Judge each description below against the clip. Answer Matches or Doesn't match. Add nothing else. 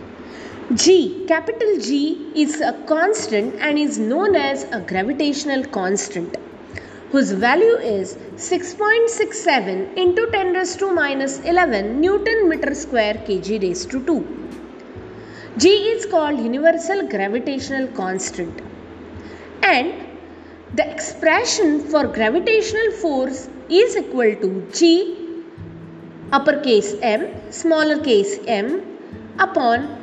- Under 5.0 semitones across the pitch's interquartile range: Doesn't match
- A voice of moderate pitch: Doesn't match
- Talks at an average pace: Doesn't match